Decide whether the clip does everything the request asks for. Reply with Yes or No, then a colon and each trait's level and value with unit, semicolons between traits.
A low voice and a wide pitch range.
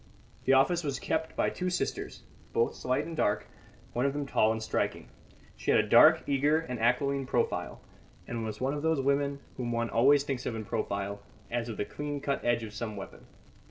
No: low, 130 Hz; average, 3.7 semitones